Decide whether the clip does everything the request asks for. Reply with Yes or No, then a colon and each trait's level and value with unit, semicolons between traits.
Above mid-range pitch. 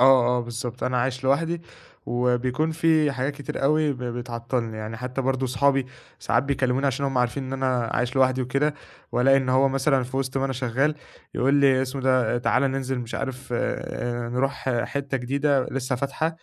No: low, 130 Hz